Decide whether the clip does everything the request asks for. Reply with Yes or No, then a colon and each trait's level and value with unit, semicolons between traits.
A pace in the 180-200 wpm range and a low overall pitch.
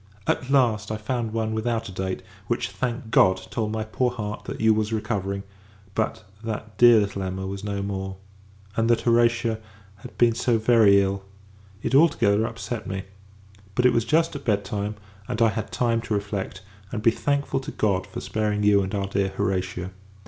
Yes: average, 190 wpm; low, 110 Hz